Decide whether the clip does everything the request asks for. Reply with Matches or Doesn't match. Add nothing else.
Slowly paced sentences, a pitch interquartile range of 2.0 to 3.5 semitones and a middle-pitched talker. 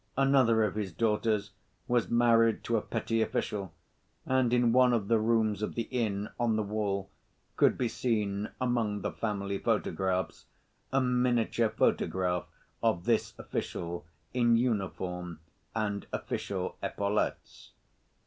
Doesn't match